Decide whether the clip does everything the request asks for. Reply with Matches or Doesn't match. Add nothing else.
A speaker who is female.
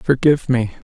Doesn't match